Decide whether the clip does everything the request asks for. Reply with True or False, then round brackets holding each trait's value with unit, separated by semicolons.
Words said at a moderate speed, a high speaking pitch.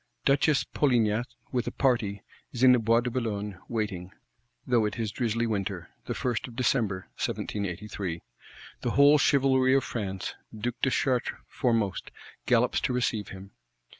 False (150 wpm; 115 Hz)